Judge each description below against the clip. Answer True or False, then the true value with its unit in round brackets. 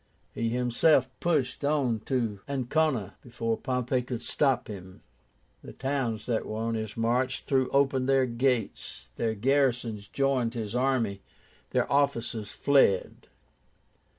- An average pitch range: True (3.1 semitones)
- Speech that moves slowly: True (130 wpm)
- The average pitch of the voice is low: True (125 Hz)